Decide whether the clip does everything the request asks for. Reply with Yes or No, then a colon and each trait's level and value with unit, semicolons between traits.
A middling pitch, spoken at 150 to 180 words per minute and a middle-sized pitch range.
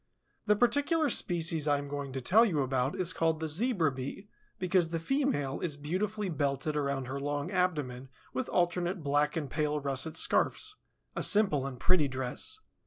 Yes: medium, 155 Hz; average, 175 wpm; average, 4.8 semitones